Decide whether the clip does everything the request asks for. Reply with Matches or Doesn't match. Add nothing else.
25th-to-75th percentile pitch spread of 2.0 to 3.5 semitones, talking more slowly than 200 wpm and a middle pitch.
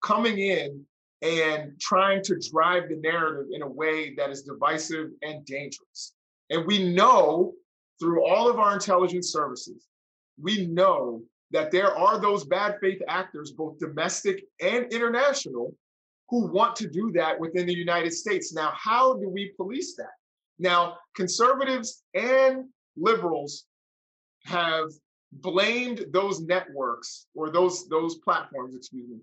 Doesn't match